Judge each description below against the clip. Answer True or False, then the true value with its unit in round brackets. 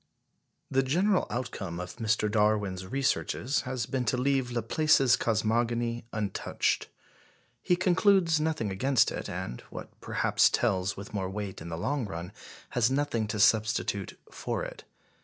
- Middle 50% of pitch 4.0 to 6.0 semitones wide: True (4.9 semitones)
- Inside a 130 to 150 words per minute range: True (140 wpm)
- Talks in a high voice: False (115 Hz)